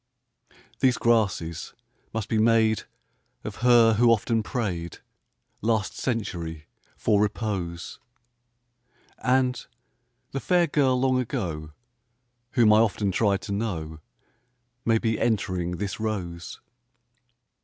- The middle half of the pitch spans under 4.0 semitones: No, average, 4.3 semitones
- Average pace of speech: No, slow, 105 wpm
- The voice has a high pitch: No, low, 110 Hz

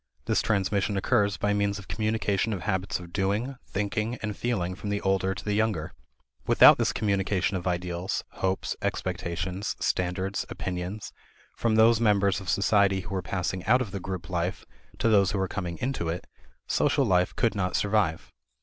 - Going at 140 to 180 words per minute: Yes, average, 175 wpm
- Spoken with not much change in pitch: Yes, narrow, 2.3 semitones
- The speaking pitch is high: No, very low, 95 Hz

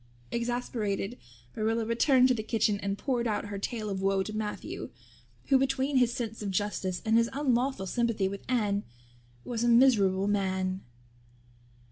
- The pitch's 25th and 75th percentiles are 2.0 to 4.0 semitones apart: Yes, average, 3.4 semitones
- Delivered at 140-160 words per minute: Yes, average, 155 wpm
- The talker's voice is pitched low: No, high, 220 Hz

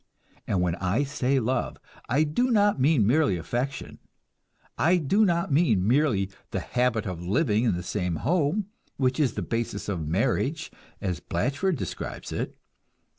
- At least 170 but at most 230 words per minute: No, average, 155 wpm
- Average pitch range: No, wide, 7.3 semitones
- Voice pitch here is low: Yes, low, 130 Hz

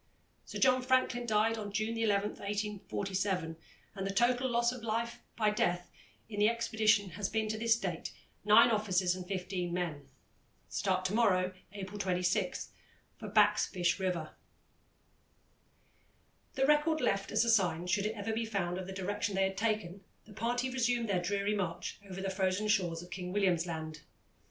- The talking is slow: No, average, 170 wpm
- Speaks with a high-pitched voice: Yes, high, 205 Hz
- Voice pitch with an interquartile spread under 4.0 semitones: Yes, average, 3.3 semitones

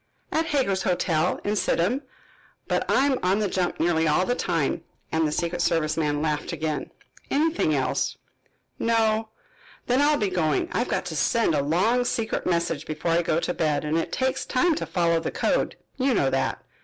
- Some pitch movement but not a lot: No, wide, 6.6 semitones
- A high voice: No, medium, 175 Hz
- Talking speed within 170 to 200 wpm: Yes, average, 190 wpm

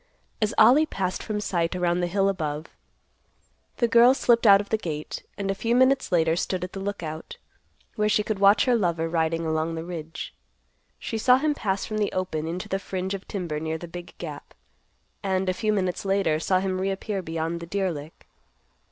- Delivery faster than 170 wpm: Yes, average, 200 wpm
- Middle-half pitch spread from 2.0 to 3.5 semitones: No, average, 3.9 semitones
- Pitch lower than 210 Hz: Yes, medium, 185 Hz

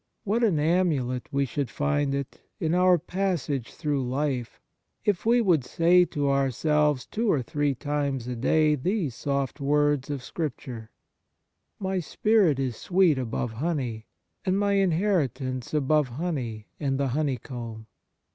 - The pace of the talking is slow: No, average, 145 wpm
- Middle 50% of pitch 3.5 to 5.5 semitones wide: Yes, average, 5.0 semitones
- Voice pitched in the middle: Yes, medium, 145 Hz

